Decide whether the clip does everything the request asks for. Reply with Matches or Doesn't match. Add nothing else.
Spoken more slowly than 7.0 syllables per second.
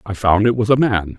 Matches